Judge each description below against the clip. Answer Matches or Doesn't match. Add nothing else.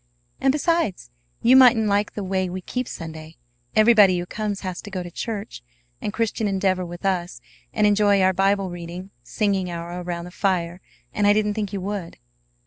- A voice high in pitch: Matches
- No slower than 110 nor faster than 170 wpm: Doesn't match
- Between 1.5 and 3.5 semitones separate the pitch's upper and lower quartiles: Matches